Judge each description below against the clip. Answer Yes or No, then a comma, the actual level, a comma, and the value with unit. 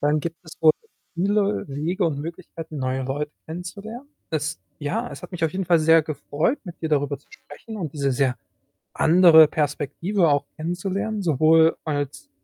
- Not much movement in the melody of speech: No, average, 3.7 semitones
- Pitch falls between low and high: Yes, medium, 160 Hz